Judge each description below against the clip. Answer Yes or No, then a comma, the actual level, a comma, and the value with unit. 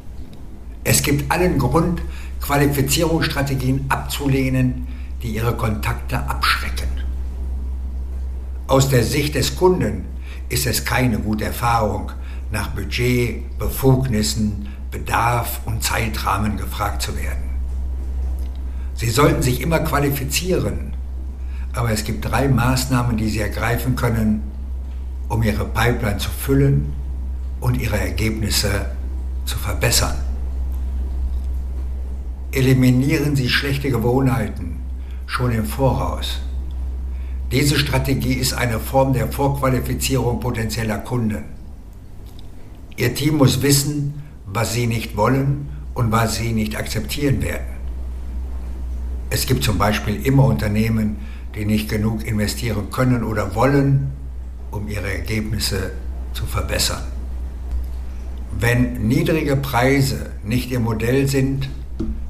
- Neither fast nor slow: No, slow, 105 wpm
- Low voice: Yes, low, 105 Hz